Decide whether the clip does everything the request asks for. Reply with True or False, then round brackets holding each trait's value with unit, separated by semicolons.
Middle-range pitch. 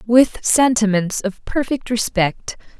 False (225 Hz)